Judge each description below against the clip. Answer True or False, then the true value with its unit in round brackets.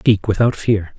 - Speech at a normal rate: True (185 wpm)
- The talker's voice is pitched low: True (105 Hz)